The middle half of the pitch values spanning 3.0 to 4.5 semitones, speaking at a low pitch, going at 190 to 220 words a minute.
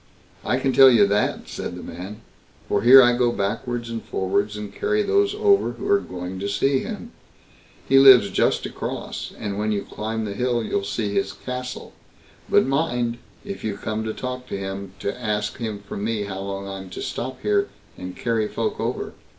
Yes: average, 4.1 semitones; low, 110 Hz; average, 195 wpm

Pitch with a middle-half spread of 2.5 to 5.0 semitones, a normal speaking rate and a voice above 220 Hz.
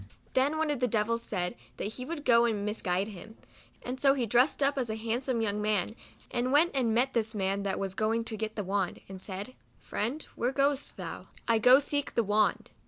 No: average, 3.9 semitones; fast, 235 wpm; high, 230 Hz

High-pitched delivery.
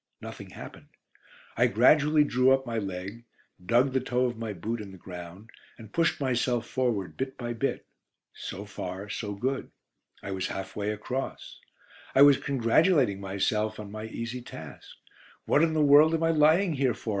No: low, 120 Hz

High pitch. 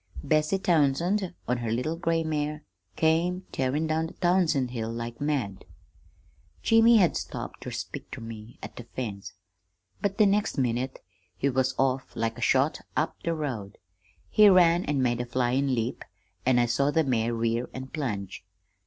No: low, 135 Hz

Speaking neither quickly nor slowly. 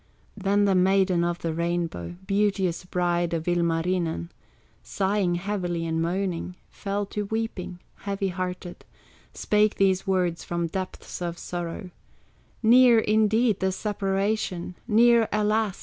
No: slow, 120 wpm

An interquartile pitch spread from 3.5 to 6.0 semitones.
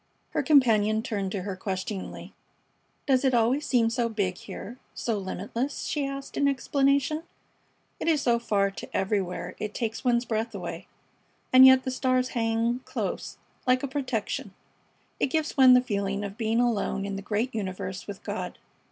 Yes: average, 4.2 semitones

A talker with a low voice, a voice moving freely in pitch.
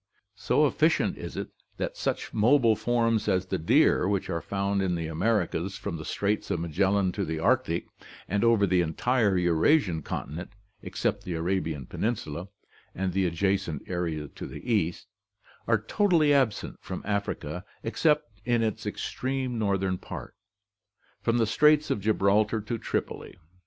No: low, 100 Hz; average, 4.7 semitones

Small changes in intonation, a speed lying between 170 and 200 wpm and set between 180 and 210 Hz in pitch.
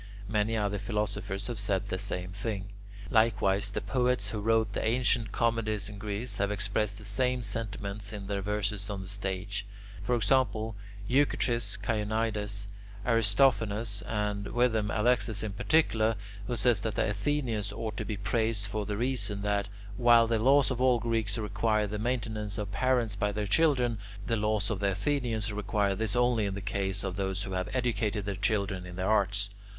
No: narrow, 2.2 semitones; average, 175 wpm; low, 105 Hz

